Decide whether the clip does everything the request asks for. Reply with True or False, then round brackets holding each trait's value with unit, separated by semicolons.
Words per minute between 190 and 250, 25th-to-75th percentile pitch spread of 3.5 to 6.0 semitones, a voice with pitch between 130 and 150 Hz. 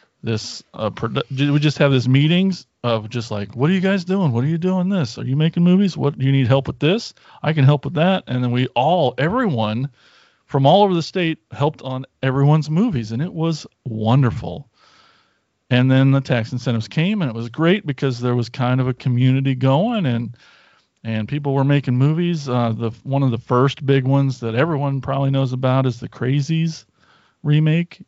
True (205 wpm; 3.8 semitones; 135 Hz)